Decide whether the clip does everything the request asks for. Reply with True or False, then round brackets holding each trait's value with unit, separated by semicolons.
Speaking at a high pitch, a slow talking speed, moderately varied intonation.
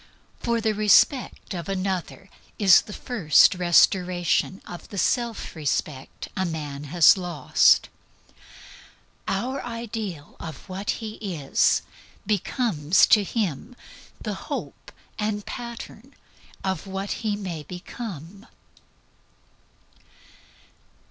True (195 Hz; 95 wpm; 4.1 semitones)